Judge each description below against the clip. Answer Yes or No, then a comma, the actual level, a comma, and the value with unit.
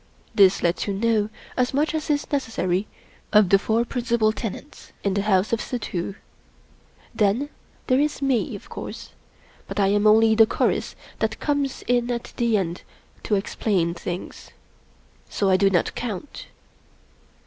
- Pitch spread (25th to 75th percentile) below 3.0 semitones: No, average, 3.9 semitones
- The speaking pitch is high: Yes, high, 215 Hz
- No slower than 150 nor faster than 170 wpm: Yes, average, 155 wpm